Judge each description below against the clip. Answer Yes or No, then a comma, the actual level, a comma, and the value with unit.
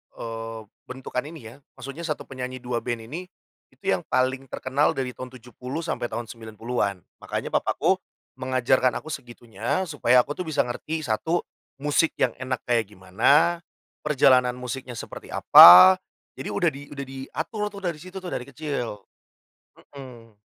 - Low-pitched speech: Yes, low, 130 Hz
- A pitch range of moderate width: Yes, average, 3.7 semitones